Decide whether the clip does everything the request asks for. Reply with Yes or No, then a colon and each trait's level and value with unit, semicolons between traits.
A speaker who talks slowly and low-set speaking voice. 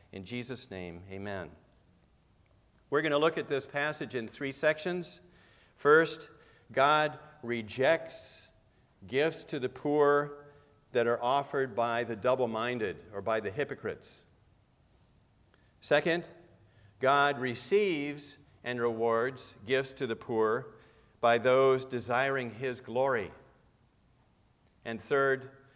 Yes: slow, 110 wpm; low, 130 Hz